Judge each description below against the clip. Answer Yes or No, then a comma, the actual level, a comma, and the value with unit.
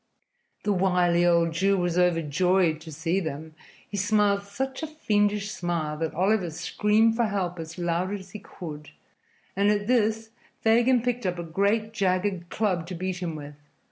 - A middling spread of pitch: Yes, average, 3.6 semitones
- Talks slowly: No, average, 170 wpm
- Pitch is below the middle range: No, medium, 185 Hz